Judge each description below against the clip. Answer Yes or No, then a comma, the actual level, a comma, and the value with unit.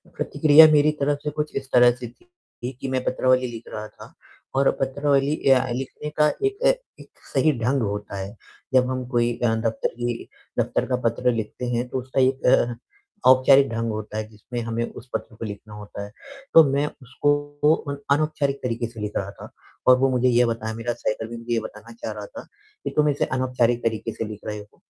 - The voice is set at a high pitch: No, low, 125 Hz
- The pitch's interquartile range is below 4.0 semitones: Yes, average, 3.1 semitones